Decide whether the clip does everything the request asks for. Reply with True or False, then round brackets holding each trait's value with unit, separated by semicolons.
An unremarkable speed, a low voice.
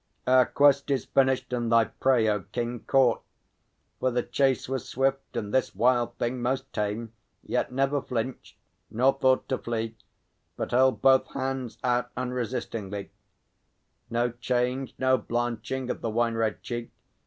True (150 wpm; 125 Hz)